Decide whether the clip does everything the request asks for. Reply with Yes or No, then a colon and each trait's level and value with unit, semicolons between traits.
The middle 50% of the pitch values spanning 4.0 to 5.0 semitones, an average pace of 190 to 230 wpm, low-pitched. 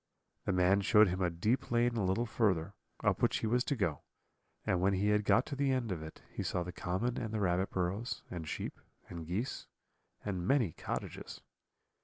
Yes: average, 4.7 semitones; fast, 205 wpm; low, 100 Hz